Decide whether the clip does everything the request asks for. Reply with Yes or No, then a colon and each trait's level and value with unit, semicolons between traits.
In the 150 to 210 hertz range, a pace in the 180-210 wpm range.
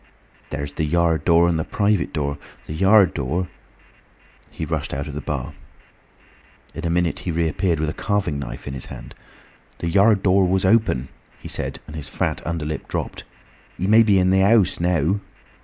No: very low, 85 Hz; average, 185 wpm